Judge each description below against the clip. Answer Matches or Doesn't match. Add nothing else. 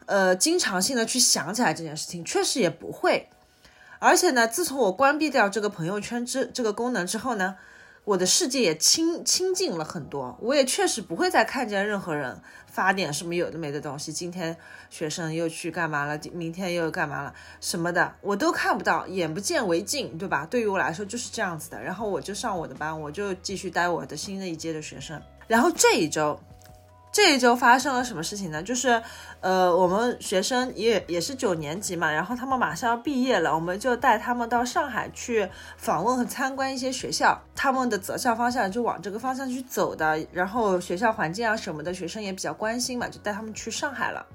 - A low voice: Doesn't match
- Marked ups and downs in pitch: Matches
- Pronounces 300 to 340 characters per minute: Matches